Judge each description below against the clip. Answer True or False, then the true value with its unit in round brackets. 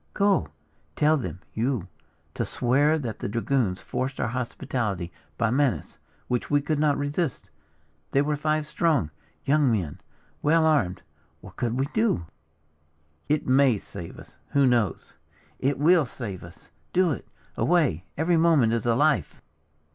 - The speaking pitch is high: False (135 Hz)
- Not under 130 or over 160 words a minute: True (145 wpm)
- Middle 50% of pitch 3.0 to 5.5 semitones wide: True (5.0 semitones)